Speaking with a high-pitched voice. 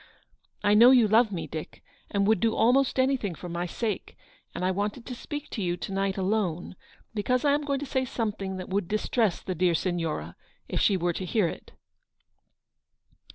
Yes: high, 205 Hz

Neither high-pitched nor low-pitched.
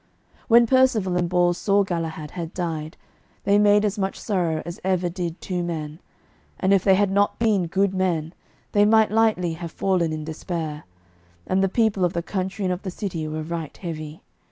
Yes: medium, 180 Hz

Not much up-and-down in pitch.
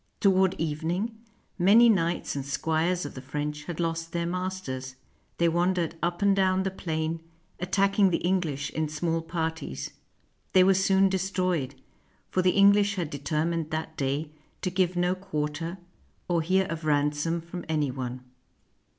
No: average, 3.3 semitones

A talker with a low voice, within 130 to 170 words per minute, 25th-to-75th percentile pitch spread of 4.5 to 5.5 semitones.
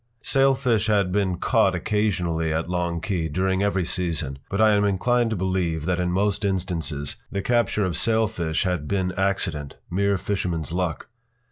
No: very low, 95 Hz; average, 160 wpm; average, 3.2 semitones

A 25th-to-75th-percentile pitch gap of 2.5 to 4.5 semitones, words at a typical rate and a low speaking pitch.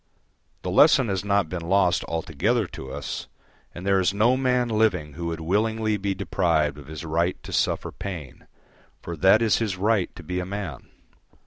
Yes: average, 4.2 semitones; average, 185 wpm; very low, 95 Hz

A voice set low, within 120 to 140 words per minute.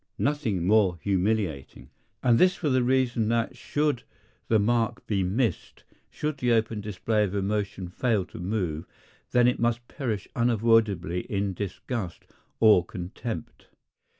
Yes: low, 110 Hz; slow, 135 wpm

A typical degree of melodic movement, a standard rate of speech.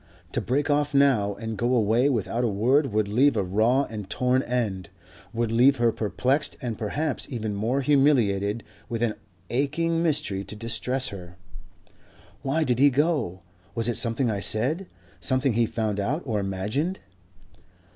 Yes: average, 4.6 semitones; average, 160 wpm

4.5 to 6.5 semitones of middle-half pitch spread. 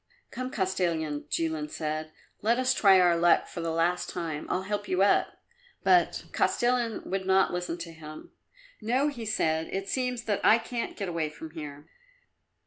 Yes: average, 5.3 semitones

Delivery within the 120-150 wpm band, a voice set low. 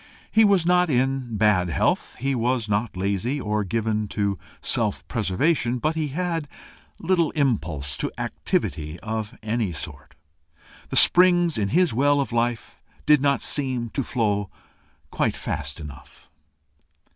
Yes: average, 140 wpm; low, 120 Hz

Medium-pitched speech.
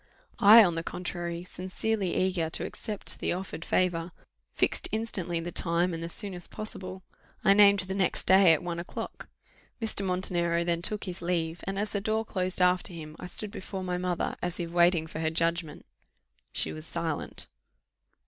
Yes: medium, 180 Hz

